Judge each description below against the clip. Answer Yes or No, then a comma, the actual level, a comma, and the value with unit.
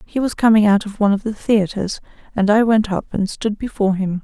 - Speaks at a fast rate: Yes, fast, 240 wpm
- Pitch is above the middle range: Yes, high, 210 Hz